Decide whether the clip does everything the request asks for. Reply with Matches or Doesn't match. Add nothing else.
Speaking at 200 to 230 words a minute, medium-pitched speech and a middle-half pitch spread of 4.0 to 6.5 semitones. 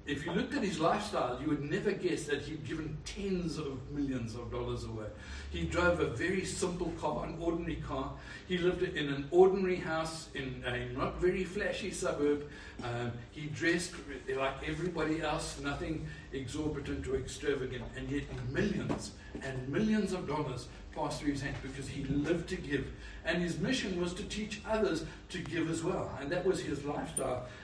Doesn't match